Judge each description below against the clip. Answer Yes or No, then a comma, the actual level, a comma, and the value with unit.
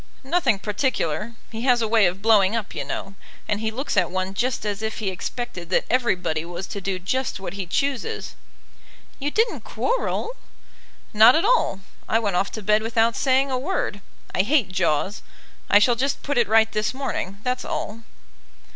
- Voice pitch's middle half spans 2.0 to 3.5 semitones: No, average, 4.6 semitones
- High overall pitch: Yes, high, 220 Hz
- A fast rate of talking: No, average, 185 wpm